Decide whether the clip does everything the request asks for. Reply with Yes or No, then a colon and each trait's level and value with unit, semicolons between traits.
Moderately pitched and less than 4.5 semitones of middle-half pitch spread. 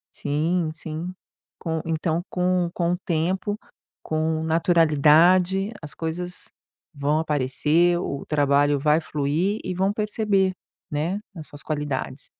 Yes: medium, 160 Hz; average, 3.2 semitones